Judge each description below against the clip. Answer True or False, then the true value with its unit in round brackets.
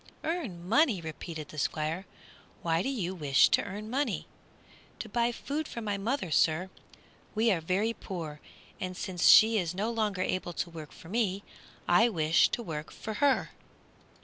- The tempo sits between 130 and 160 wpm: False (170 wpm)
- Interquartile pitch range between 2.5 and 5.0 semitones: False (5.4 semitones)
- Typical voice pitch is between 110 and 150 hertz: False (190 Hz)